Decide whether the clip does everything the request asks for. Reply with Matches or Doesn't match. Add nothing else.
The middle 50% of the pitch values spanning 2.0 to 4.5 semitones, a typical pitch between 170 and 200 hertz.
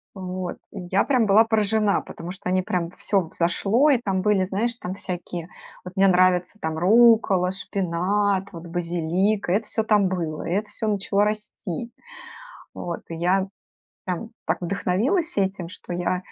Matches